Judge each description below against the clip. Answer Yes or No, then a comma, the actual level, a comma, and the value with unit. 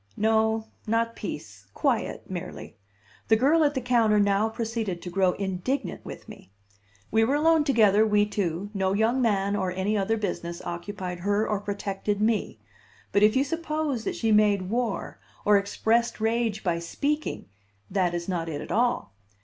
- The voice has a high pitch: Yes, high, 210 Hz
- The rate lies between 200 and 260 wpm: No, average, 165 wpm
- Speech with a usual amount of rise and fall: Yes, average, 3.2 semitones